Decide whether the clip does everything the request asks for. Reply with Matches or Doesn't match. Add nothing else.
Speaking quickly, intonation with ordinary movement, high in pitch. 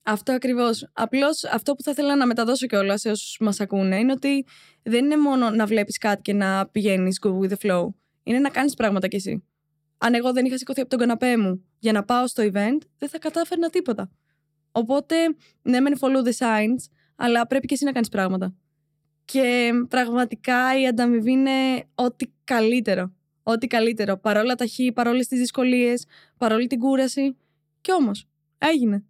Matches